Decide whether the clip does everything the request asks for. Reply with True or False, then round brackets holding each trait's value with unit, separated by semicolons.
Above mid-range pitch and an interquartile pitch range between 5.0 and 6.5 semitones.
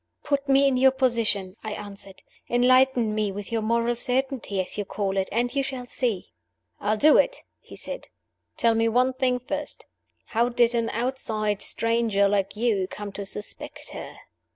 False (230 Hz; 3.7 semitones)